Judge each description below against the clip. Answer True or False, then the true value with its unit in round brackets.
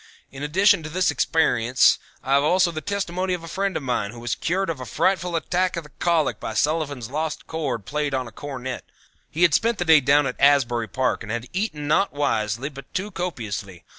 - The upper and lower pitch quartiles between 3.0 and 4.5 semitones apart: False (5.5 semitones)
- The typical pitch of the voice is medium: True (150 Hz)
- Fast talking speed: True (215 wpm)